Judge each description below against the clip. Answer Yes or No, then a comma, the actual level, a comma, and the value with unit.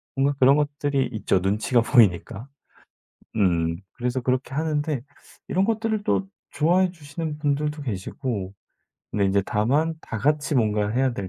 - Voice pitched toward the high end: No, low, 135 Hz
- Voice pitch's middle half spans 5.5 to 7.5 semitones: Yes, wide, 6.0 semitones